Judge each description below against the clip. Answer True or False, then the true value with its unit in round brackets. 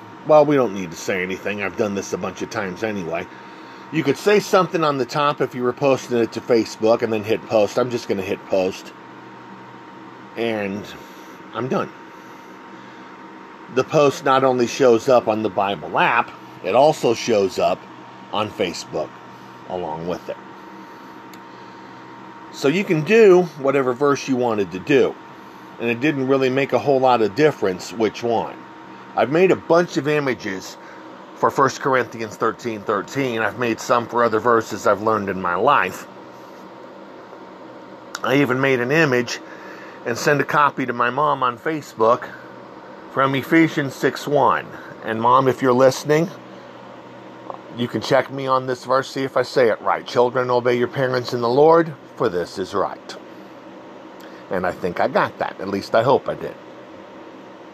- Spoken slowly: False (170 wpm)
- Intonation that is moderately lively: False (5.9 semitones)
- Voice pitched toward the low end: True (120 Hz)